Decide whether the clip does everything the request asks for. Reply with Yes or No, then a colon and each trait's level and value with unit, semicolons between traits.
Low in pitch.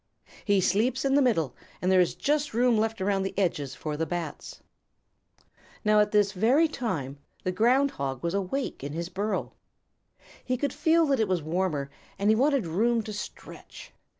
No: high, 205 Hz